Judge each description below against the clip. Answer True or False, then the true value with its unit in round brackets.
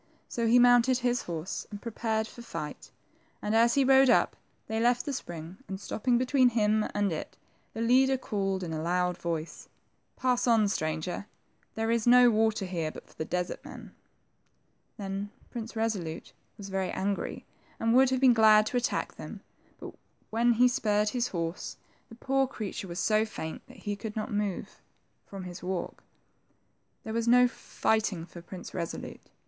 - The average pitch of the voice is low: False (215 Hz)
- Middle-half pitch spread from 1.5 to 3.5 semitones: False (4.3 semitones)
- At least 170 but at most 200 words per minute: True (175 wpm)